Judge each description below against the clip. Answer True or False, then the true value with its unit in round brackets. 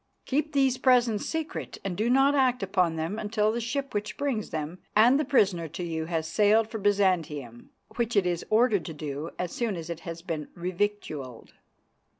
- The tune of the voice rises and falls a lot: True (6.3 semitones)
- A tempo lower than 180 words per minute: False (185 wpm)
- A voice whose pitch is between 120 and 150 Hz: False (205 Hz)